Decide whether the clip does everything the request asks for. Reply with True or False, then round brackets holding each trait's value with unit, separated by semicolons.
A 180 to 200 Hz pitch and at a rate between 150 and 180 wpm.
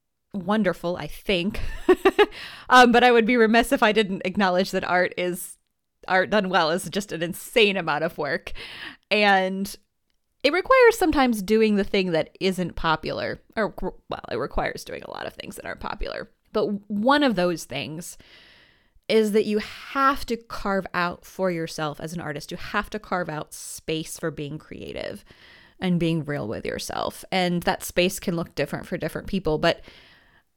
True (190 Hz; 175 wpm)